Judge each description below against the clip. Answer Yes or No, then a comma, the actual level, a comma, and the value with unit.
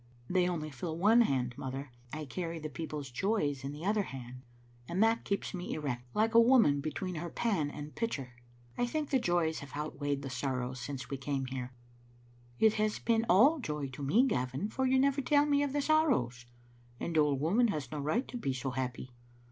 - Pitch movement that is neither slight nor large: No, wide, 8.5 semitones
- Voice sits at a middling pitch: Yes, medium, 155 Hz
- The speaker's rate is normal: No, fast, 210 wpm